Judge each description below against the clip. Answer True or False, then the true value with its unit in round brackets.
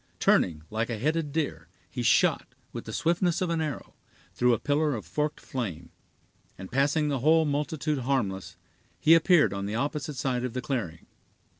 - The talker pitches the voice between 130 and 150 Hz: True (140 Hz)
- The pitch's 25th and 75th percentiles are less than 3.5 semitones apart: False (4.9 semitones)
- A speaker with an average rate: True (175 wpm)